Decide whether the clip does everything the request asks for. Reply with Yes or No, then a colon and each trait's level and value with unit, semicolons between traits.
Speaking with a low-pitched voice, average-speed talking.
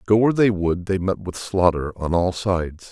No: very low, 90 Hz; fast, 225 wpm